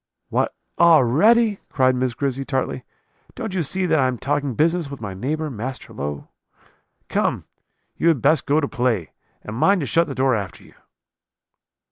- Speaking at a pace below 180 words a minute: Yes, average, 170 wpm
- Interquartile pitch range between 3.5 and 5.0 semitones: Yes, average, 4.6 semitones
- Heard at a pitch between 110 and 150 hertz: Yes, medium, 140 Hz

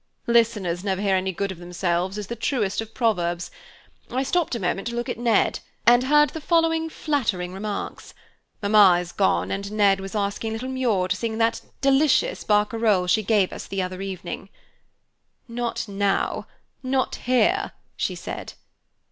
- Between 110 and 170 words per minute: Yes, average, 165 wpm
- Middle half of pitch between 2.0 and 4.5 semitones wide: Yes, average, 4.1 semitones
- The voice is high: Yes, high, 210 Hz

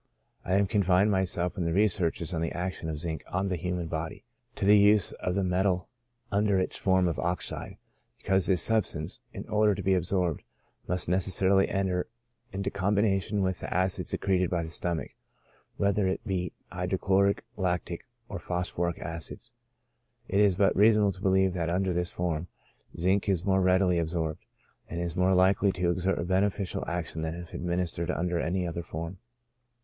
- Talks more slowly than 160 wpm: No, average, 175 wpm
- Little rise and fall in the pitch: Yes, narrow, 2.0 semitones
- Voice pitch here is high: No, very low, 90 Hz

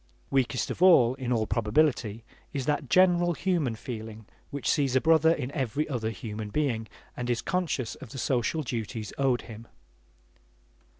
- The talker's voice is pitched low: Yes, low, 125 Hz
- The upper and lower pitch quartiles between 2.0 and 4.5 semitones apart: No, average, 5.1 semitones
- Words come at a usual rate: Yes, average, 160 wpm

